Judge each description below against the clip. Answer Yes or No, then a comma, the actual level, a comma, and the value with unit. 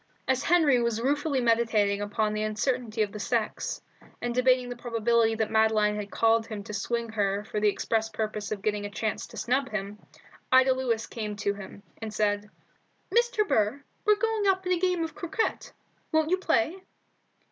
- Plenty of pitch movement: No, average, 3.9 semitones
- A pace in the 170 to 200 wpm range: Yes, average, 180 wpm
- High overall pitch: Yes, high, 225 Hz